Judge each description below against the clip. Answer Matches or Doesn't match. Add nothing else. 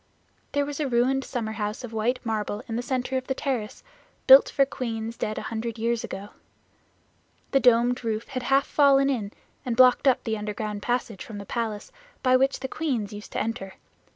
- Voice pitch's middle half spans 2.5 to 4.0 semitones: Matches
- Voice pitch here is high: Matches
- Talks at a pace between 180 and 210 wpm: Matches